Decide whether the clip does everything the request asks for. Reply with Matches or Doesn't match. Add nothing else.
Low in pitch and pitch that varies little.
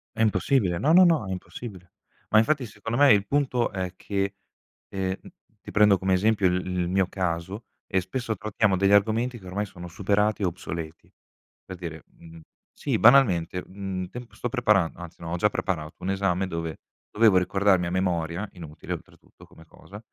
Doesn't match